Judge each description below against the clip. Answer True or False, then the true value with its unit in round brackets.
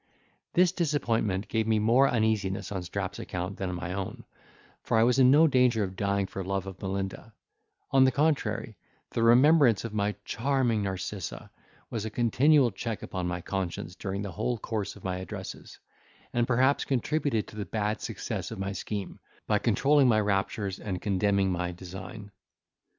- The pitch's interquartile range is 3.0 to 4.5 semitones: True (3.9 semitones)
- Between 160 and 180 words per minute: True (170 wpm)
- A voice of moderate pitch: False (105 Hz)